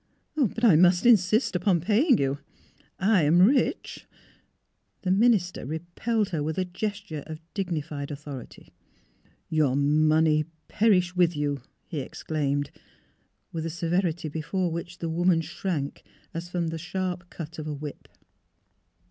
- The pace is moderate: Yes, average, 150 wpm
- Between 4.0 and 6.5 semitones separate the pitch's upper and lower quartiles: No, average, 3.4 semitones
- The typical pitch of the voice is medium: Yes, medium, 170 Hz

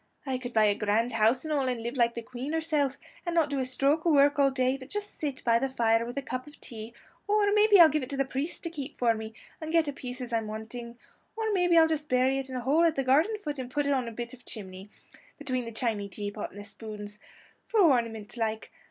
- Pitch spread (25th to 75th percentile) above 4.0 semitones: Yes, average, 4.4 semitones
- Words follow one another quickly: Yes, fast, 265 wpm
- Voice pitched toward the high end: Yes, very high, 260 Hz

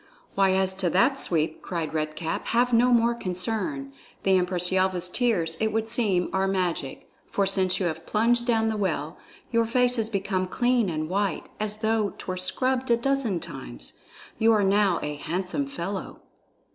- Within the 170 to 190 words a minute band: Yes, average, 175 wpm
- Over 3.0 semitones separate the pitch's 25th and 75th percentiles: Yes, average, 4.3 semitones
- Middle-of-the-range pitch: No, high, 195 Hz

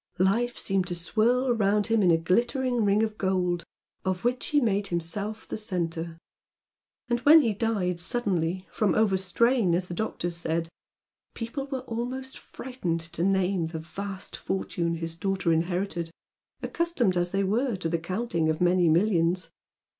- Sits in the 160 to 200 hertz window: Yes, high, 190 Hz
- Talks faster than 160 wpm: No, average, 155 wpm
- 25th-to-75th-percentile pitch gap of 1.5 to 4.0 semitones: No, average, 4.8 semitones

